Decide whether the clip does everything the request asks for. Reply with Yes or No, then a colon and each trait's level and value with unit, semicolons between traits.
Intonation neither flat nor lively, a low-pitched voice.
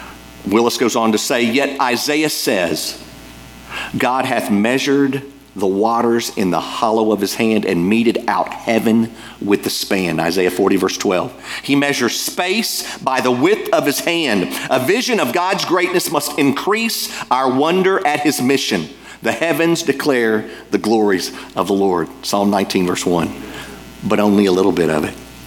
No: wide, 6.0 semitones; low, 120 Hz